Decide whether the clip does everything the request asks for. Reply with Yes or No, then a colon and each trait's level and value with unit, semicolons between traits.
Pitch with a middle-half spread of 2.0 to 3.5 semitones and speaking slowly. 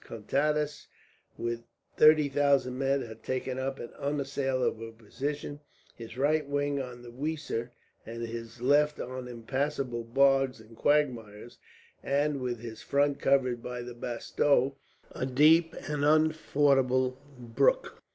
Yes: average, 3.1 semitones; slow, 125 wpm